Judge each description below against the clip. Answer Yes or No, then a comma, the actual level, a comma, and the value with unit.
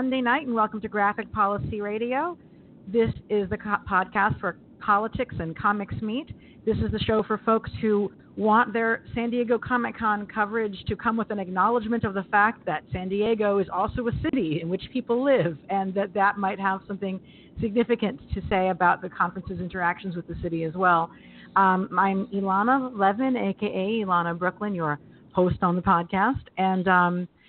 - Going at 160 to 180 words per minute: Yes, average, 175 wpm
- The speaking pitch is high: Yes, high, 200 Hz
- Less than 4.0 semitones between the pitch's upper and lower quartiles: Yes, average, 3.1 semitones